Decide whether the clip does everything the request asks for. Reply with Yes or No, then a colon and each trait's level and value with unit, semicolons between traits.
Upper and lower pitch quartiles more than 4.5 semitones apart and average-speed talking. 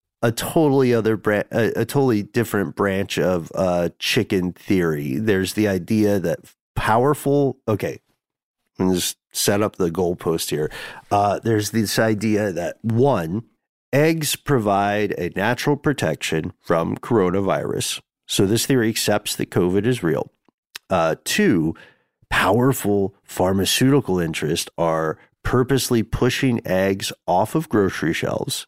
No: average, 4.9 semitones; slow, 125 wpm